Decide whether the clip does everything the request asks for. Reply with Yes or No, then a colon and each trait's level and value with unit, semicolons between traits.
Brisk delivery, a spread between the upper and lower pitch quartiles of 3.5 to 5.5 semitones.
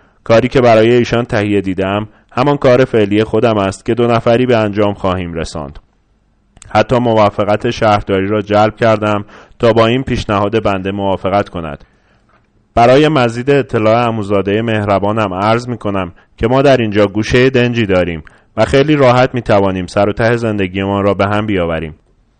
No: fast, 160 wpm; average, 2.9 semitones